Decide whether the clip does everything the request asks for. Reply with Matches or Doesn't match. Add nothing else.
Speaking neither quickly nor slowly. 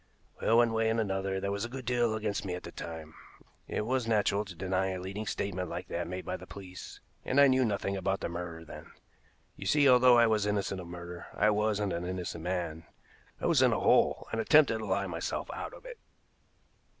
Doesn't match